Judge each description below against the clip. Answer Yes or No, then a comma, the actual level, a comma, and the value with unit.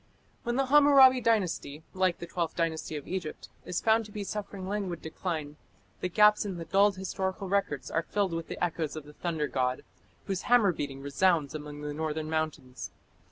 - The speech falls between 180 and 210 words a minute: Yes, average, 185 wpm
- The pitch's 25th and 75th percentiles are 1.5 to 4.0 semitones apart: No, average, 4.5 semitones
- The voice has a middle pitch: Yes, medium, 175 Hz